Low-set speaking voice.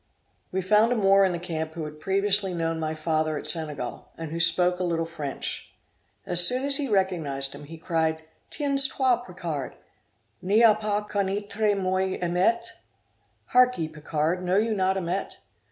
No: medium, 180 Hz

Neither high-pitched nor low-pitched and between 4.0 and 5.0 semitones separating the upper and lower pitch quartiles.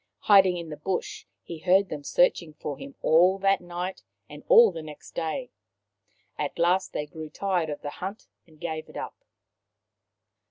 No: medium, 170 Hz; average, 3.5 semitones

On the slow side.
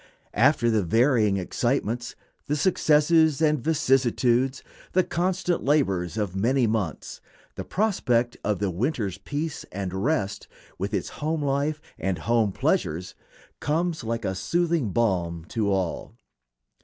Yes: slow, 130 wpm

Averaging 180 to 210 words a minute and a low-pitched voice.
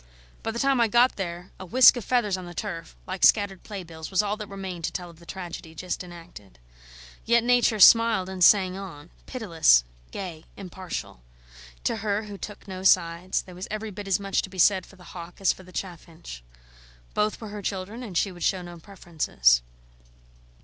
No: average, 200 wpm; high, 190 Hz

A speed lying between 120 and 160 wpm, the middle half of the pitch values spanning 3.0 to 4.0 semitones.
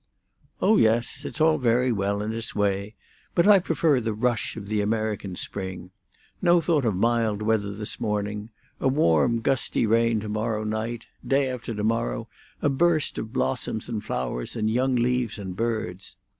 No: average, 170 wpm; average, 3.3 semitones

